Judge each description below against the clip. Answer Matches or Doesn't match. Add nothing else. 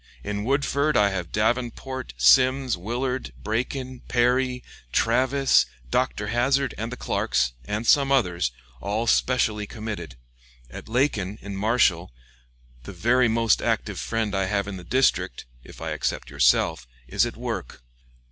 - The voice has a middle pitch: Doesn't match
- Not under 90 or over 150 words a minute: Matches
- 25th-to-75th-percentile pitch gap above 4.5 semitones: Matches